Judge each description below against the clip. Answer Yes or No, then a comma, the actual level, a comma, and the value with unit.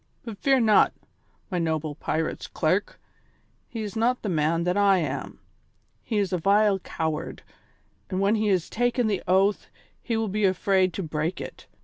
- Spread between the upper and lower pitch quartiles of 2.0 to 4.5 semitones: Yes, average, 4.0 semitones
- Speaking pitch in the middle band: No, high, 195 Hz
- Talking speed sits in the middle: Yes, average, 170 wpm